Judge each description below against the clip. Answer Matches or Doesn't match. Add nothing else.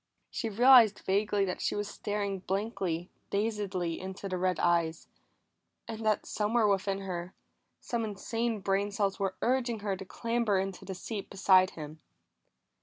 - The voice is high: Matches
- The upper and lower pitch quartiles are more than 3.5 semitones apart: Doesn't match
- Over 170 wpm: Doesn't match